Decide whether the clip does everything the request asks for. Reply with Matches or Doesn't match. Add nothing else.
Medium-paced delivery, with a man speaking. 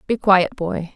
Doesn't match